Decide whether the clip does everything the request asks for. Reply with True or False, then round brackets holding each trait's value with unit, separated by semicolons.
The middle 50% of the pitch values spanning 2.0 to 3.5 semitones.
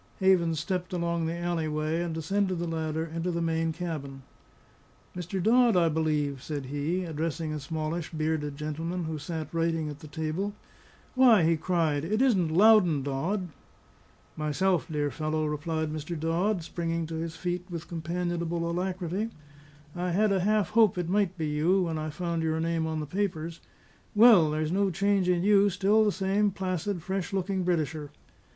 True (2.9 semitones)